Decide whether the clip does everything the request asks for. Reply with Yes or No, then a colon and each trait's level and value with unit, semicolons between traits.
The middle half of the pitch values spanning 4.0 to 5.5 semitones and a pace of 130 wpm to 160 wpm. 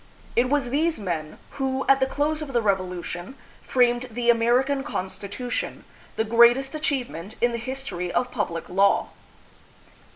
Yes: average, 5.1 semitones; average, 140 wpm